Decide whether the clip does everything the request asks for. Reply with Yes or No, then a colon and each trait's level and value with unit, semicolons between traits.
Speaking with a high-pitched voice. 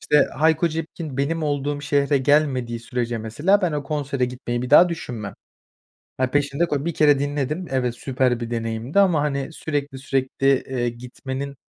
No: medium, 140 Hz